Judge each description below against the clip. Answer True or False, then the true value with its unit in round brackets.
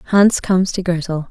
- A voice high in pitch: False (180 Hz)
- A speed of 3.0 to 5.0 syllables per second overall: True (4.8 syllables/s)